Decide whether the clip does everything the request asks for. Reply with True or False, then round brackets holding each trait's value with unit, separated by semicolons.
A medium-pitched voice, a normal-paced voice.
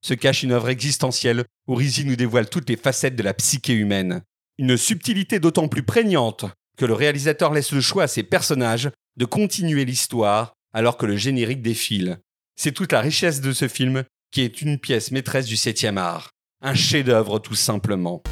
False (130 Hz; 185 wpm)